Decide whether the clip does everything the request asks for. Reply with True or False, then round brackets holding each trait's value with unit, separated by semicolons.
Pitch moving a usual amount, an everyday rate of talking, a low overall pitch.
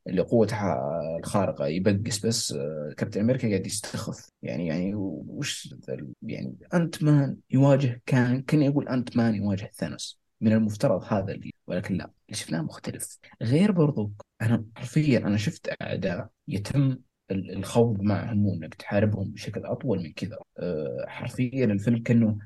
False (3.8 semitones; 140 wpm; 115 Hz)